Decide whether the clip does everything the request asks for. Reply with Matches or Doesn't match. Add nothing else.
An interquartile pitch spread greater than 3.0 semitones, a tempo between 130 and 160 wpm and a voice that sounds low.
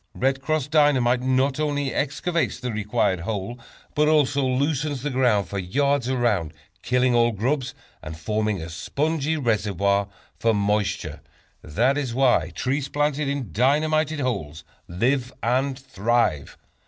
Matches